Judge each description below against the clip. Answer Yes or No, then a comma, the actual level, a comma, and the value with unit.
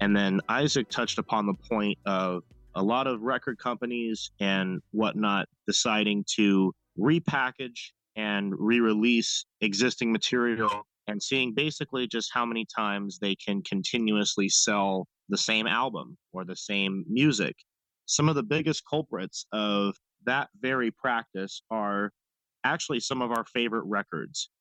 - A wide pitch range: No, average, 3.4 semitones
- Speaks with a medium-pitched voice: No, low, 110 Hz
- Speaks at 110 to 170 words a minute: Yes, average, 140 wpm